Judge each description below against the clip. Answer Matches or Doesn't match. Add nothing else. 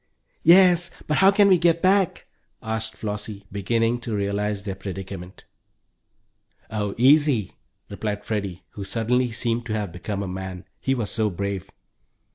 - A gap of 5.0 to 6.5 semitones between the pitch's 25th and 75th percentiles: Doesn't match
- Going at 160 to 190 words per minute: Doesn't match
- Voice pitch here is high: Doesn't match